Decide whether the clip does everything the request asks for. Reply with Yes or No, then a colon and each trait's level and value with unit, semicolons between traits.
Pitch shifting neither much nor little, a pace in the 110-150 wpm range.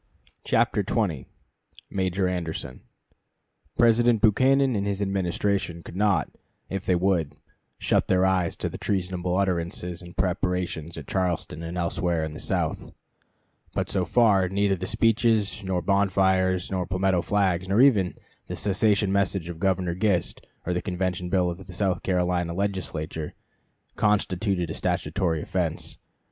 No: narrow, 2.2 semitones; average, 140 wpm